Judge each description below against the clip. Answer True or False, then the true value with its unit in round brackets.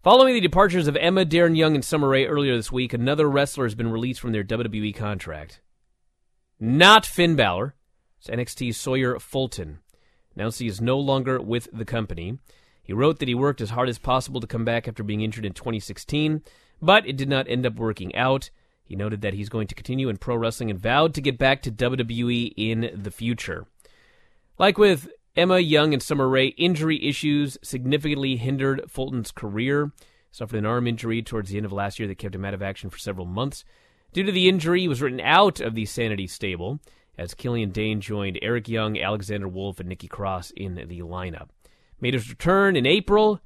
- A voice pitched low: True (120 Hz)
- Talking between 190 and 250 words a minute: True (200 wpm)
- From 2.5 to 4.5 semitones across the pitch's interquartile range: False (5.2 semitones)